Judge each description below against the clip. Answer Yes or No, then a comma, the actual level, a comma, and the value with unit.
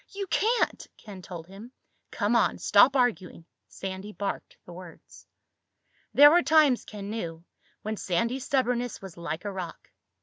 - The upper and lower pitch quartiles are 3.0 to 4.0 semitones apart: No, average, 5.3 semitones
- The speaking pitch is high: Yes, high, 210 Hz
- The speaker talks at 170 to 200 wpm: No, average, 145 wpm